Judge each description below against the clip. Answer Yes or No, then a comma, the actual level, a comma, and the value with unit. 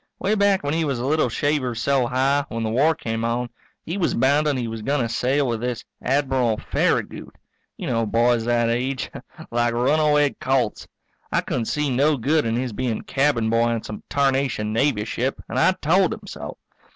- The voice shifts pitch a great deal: No, average, 3.8 semitones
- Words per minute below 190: No, average, 195 wpm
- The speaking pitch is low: Yes, low, 130 Hz